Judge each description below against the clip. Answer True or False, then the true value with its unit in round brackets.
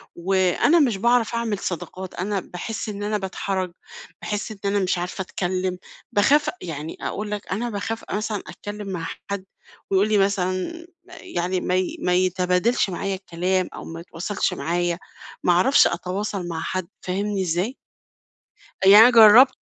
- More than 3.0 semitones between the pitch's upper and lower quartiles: False (2.6 semitones)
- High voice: True (195 Hz)